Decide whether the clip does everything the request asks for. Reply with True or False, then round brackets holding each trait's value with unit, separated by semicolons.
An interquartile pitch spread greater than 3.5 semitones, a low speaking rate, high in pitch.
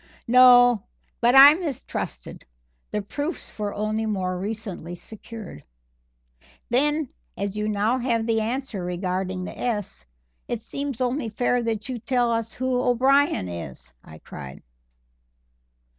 True (4.1 semitones; 130 wpm; 225 Hz)